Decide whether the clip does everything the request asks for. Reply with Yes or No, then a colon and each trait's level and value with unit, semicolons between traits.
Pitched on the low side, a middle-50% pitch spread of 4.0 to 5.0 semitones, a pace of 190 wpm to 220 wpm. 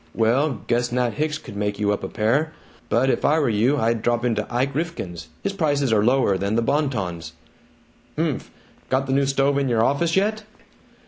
Yes: low, 125 Hz; average, 4.4 semitones; average, 200 wpm